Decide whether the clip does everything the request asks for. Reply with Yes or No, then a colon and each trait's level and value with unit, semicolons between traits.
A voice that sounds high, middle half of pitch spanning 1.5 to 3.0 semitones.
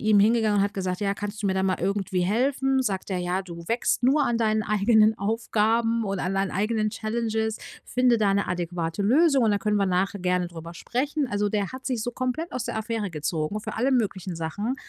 No: high, 210 Hz; average, 3.4 semitones